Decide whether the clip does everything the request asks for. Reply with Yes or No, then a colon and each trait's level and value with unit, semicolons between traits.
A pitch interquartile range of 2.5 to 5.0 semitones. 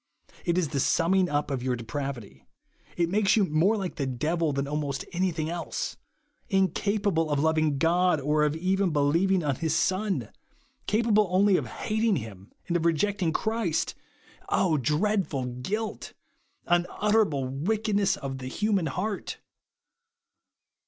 No: wide, 5.4 semitones